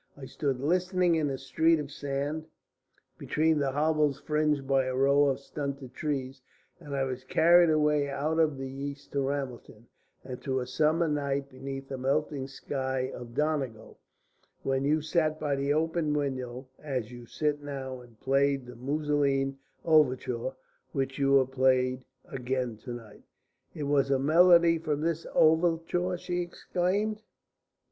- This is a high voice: No, medium, 140 Hz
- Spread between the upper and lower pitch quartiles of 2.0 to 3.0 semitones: Yes, average, 2.7 semitones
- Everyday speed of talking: Yes, average, 155 wpm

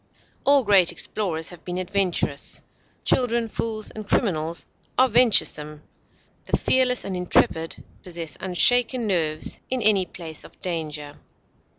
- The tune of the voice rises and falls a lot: Yes, wide, 5.8 semitones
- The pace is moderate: No, slow, 120 wpm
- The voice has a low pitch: No, medium, 185 Hz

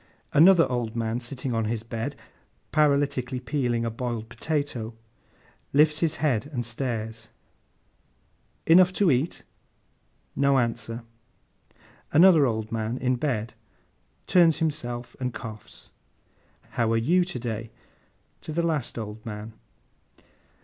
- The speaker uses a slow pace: Yes, slow, 120 wpm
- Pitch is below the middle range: Yes, low, 125 Hz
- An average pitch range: Yes, average, 4.8 semitones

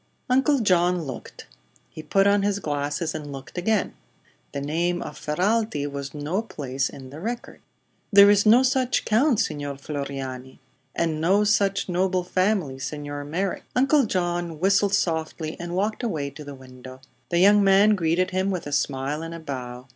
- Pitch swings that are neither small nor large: No, wide, 5.7 semitones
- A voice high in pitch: No, medium, 170 Hz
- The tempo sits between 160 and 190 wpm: Yes, average, 170 wpm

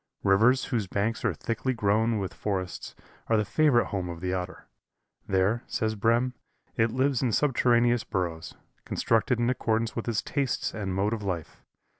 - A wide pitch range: No, average, 3.5 semitones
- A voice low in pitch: Yes, low, 110 Hz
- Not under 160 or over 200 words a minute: Yes, average, 165 wpm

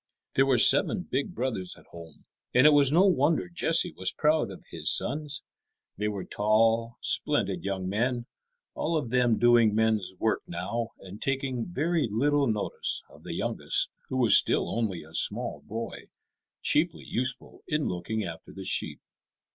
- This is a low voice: Yes, low, 120 Hz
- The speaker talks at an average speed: Yes, average, 165 wpm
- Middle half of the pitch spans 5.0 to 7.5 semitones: Yes, wide, 5.4 semitones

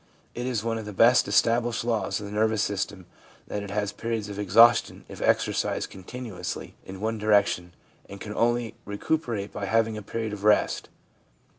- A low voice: Yes, low, 110 Hz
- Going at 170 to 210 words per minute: Yes, average, 175 wpm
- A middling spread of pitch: No, narrow, 2.2 semitones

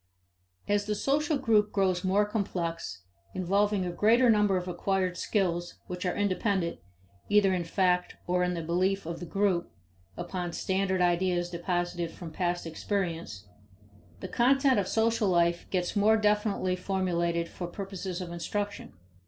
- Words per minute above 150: No, average, 145 wpm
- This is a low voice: No, medium, 185 Hz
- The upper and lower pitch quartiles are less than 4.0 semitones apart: Yes, average, 2.8 semitones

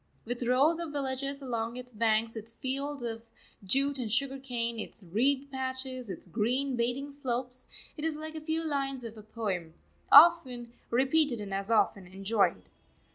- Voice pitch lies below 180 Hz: No, very high, 250 Hz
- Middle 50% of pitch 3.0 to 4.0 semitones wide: Yes, average, 3.6 semitones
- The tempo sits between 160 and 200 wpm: Yes, average, 165 wpm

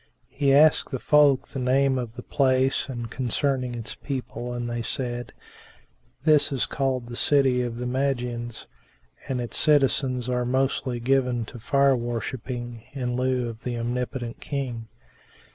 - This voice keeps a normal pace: Yes, average, 150 wpm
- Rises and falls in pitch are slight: Yes, narrow, 2.0 semitones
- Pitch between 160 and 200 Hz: No, low, 125 Hz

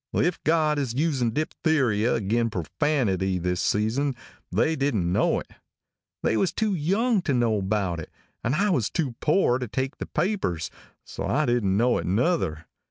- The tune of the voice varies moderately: No, wide, 7.1 semitones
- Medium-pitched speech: No, low, 125 Hz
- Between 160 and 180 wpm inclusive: Yes, average, 165 wpm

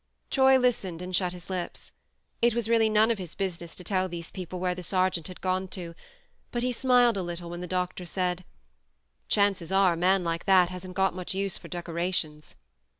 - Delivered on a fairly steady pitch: Yes, narrow, 2.0 semitones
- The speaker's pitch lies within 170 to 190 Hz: Yes, medium, 185 Hz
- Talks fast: Yes, fast, 210 wpm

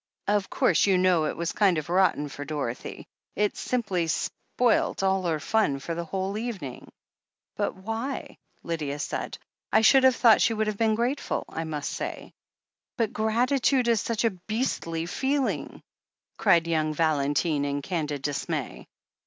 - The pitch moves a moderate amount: No, wide, 6.1 semitones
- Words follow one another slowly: No, average, 160 wpm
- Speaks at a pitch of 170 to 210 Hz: Yes, medium, 185 Hz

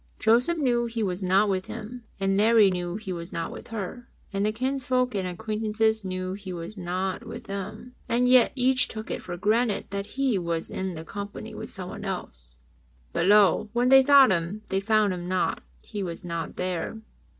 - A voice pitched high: Yes, high, 205 Hz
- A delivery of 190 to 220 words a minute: Yes, average, 195 wpm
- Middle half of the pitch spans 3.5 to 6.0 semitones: Yes, average, 4.0 semitones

